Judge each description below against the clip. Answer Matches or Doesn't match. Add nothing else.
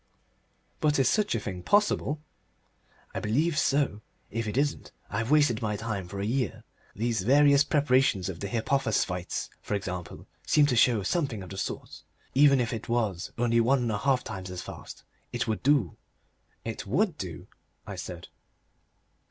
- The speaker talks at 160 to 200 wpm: Matches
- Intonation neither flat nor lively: Doesn't match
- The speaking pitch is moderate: Doesn't match